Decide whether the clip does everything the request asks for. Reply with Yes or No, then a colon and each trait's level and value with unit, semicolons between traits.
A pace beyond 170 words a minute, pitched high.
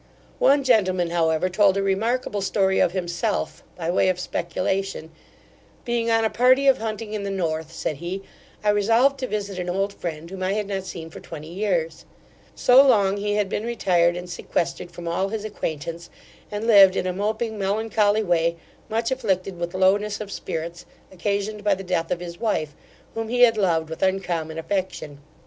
Yes: average, 185 wpm; high, 195 Hz